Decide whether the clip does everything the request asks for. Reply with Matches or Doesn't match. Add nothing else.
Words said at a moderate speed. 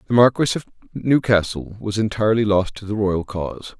Matches